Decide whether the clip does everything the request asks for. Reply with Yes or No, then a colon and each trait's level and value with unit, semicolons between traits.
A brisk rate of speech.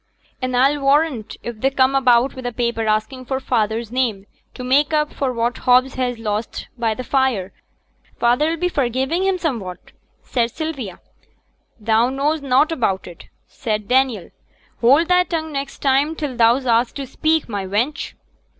No: average, 170 wpm